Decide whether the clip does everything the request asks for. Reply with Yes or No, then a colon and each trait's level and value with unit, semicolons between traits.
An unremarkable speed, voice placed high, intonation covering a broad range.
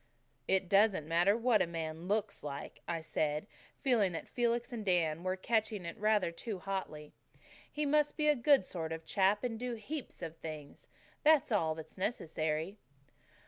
Yes: average, 170 wpm; high, 195 Hz; wide, 6.0 semitones